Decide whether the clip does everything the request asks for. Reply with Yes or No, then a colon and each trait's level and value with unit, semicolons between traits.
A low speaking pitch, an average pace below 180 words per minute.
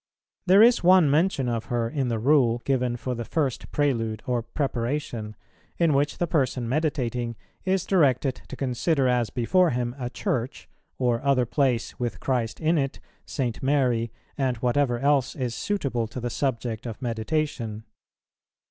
Yes: low, 125 Hz; average, 155 wpm